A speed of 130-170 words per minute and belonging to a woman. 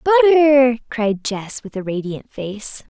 Yes: average, 140 wpm; female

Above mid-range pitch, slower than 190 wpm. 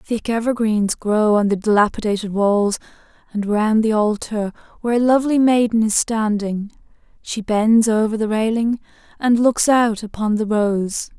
Yes: high, 220 Hz; average, 150 wpm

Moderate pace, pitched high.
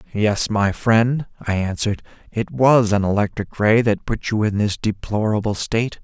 No: average, 170 wpm; low, 105 Hz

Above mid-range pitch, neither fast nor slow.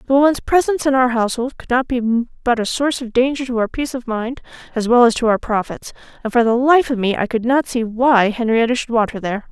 No: high, 240 Hz; fast, 260 wpm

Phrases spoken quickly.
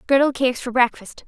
No: average, 190 wpm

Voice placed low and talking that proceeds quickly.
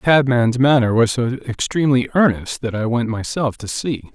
No: low, 125 Hz; average, 190 wpm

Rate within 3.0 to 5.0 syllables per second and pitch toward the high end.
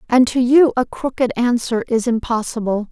Yes: 4.9 syllables/s; high, 240 Hz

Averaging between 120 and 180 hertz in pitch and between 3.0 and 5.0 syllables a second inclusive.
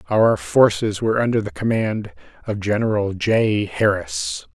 No: low, 110 Hz; 4.3 syllables/s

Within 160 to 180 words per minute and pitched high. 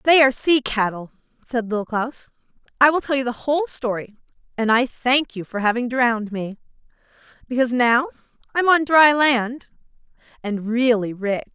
Yes: average, 165 wpm; high, 245 Hz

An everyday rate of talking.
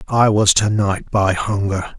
Yes: average, 180 wpm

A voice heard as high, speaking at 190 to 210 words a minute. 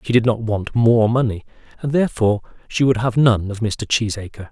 No: low, 115 Hz; average, 200 wpm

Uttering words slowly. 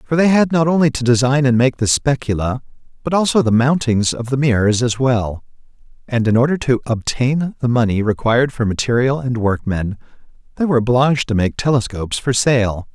No: average, 185 wpm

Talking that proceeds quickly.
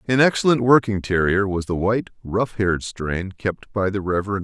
No: average, 190 wpm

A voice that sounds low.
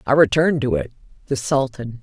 Yes: low, 130 Hz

